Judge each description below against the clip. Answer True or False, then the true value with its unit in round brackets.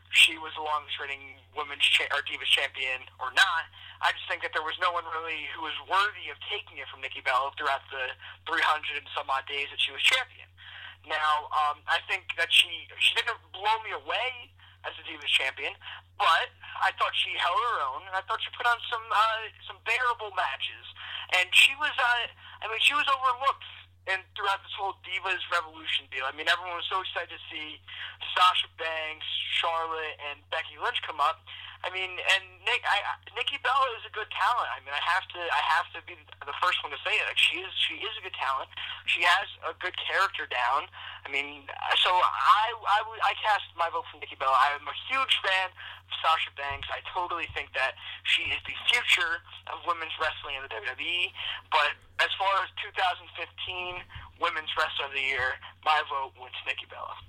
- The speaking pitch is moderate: True (170 Hz)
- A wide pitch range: True (7.4 semitones)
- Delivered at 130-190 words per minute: False (200 wpm)